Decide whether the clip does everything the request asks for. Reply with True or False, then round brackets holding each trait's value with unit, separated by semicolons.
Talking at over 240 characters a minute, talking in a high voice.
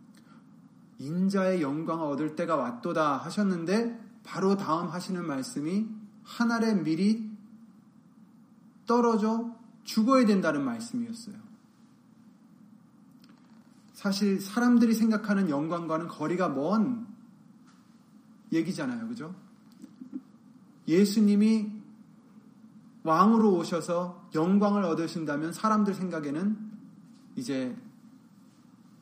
False (205 characters per minute; 220 Hz)